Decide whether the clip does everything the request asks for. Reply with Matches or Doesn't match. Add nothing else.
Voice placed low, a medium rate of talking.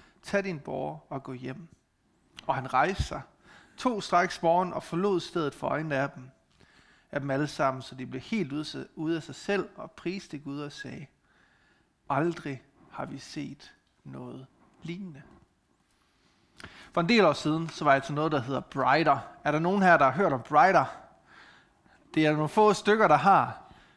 Doesn't match